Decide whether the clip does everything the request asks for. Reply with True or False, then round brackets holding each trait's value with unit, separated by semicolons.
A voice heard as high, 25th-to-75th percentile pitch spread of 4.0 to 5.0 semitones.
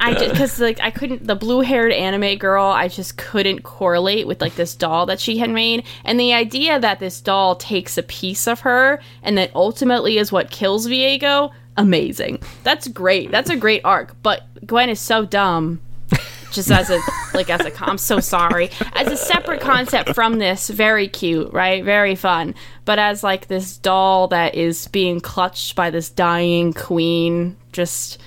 True (195 Hz; 4.4 semitones)